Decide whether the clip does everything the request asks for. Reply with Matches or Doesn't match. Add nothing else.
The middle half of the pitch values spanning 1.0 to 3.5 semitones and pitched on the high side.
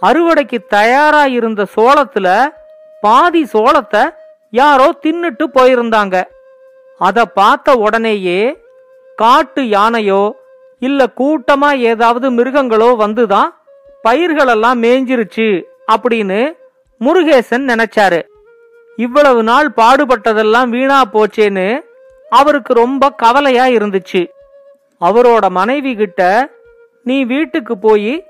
Doesn't match